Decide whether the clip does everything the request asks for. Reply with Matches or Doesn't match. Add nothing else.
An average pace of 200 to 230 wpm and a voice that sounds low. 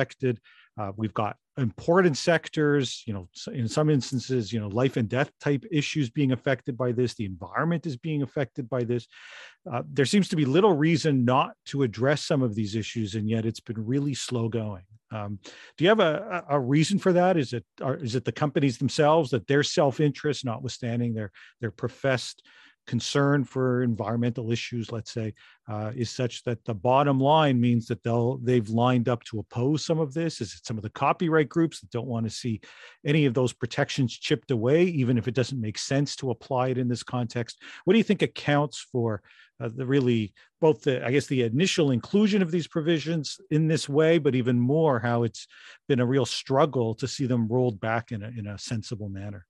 Matches